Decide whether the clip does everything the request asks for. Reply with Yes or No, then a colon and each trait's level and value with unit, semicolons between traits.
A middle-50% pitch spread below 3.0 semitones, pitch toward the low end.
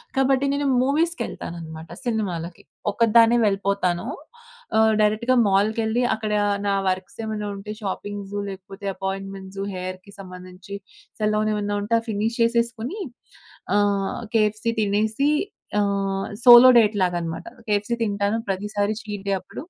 No: narrow, 2.5 semitones; high, 205 Hz